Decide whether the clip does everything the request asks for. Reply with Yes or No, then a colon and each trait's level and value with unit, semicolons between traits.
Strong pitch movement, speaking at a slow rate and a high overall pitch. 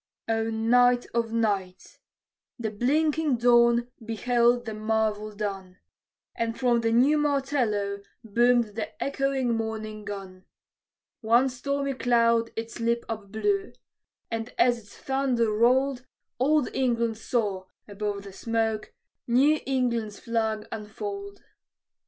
No: narrow, 2.6 semitones; slow, 115 wpm; high, 230 Hz